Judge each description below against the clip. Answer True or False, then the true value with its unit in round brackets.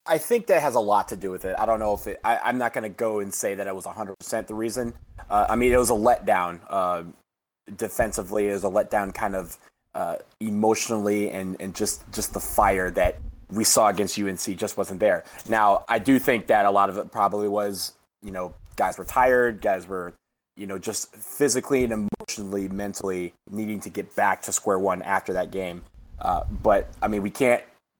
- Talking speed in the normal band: False (215 wpm)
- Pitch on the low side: True (100 Hz)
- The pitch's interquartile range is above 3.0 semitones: False (2.6 semitones)